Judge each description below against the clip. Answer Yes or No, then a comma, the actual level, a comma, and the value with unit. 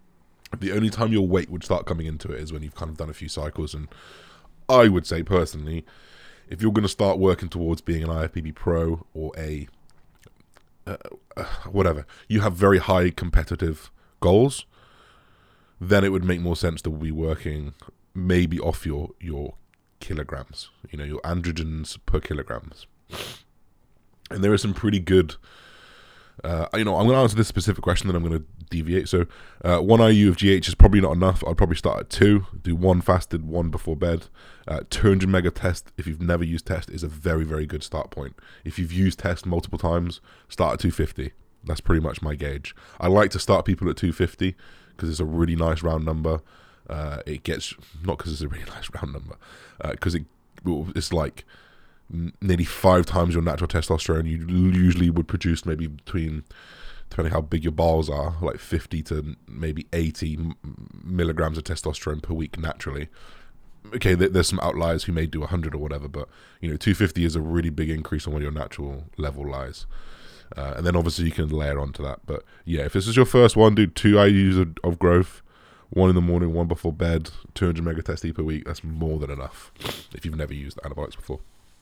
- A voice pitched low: Yes, very low, 85 Hz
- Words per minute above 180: Yes, average, 195 wpm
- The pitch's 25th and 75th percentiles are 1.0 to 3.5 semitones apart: Yes, average, 2.9 semitones